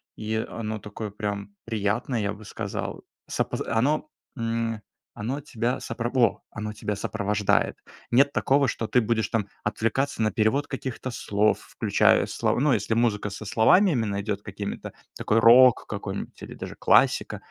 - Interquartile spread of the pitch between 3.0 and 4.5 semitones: No, narrow, 2.6 semitones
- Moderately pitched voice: No, low, 110 Hz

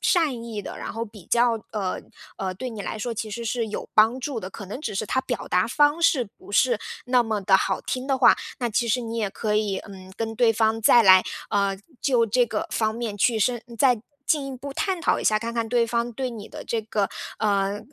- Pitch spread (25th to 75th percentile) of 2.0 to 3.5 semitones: Yes, average, 2.9 semitones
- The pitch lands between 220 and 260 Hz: Yes, high, 225 Hz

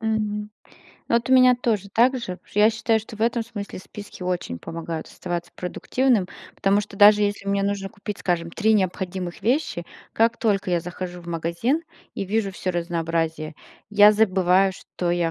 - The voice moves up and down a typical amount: Yes, average, 3.7 semitones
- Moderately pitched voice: No, high, 200 Hz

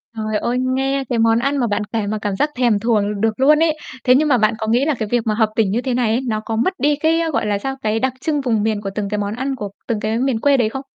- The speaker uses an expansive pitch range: No, average, 3.8 semitones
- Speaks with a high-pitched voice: Yes, high, 230 Hz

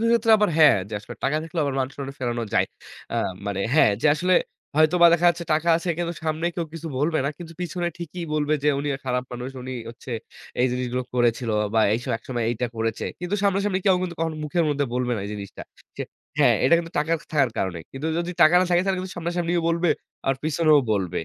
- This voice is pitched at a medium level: Yes, medium, 155 Hz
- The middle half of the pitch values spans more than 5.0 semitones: Yes, wide, 5.4 semitones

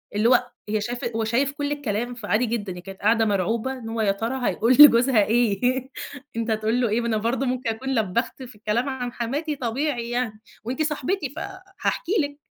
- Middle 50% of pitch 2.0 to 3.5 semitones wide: Yes, average, 3.2 semitones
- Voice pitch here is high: Yes, high, 240 Hz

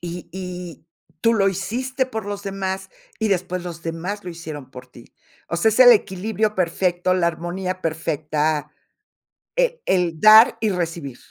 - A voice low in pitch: No, medium, 185 Hz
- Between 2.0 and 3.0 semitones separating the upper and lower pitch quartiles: No, average, 3.6 semitones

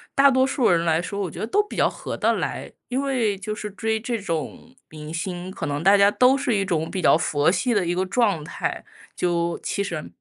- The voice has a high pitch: Yes, high, 195 Hz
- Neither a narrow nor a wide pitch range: No, wide, 5.8 semitones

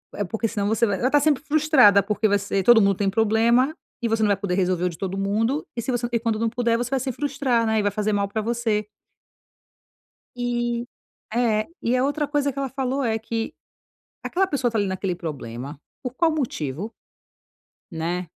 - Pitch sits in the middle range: No, high, 225 Hz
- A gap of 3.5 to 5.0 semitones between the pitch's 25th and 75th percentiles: Yes, average, 3.9 semitones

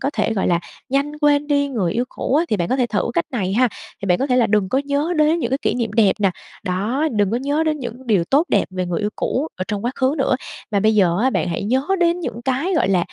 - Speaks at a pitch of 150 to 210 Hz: No, high, 245 Hz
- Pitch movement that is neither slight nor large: No, wide, 5.9 semitones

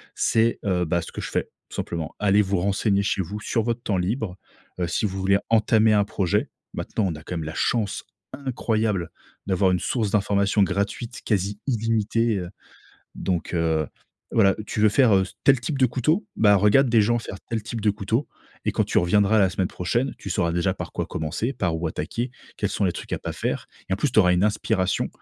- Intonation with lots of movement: No, average, 3.6 semitones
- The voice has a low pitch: Yes, low, 100 Hz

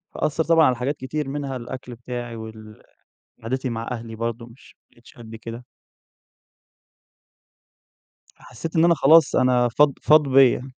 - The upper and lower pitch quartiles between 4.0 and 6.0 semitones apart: No, average, 3.3 semitones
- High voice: No, low, 125 Hz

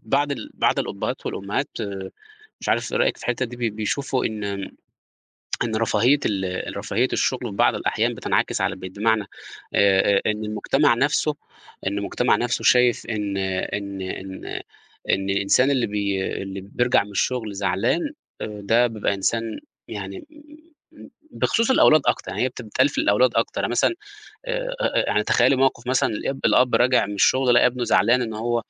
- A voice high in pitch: No, low, 115 Hz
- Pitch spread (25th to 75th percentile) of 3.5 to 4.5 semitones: Yes, average, 3.9 semitones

